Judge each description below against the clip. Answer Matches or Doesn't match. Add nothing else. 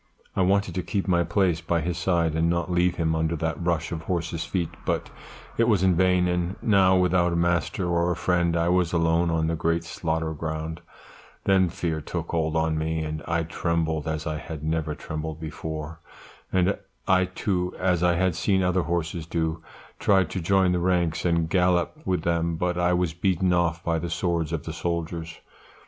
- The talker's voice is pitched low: Matches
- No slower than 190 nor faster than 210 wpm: Matches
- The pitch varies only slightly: Matches